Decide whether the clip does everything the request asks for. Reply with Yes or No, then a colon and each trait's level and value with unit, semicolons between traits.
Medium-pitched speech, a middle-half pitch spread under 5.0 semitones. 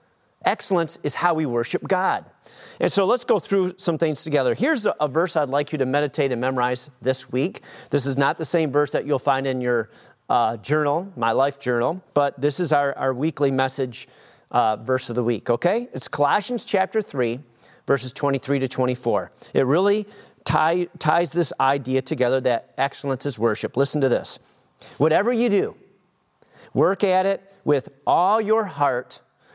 Yes: medium, 145 Hz; average, 4.6 semitones